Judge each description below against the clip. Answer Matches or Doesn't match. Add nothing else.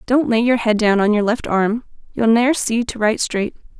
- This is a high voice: Matches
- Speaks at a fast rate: Matches